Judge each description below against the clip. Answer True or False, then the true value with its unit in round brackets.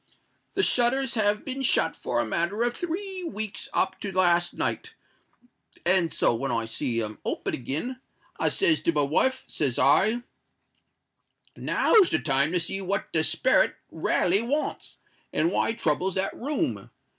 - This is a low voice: False (195 Hz)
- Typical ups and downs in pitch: False (8.7 semitones)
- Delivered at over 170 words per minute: False (160 wpm)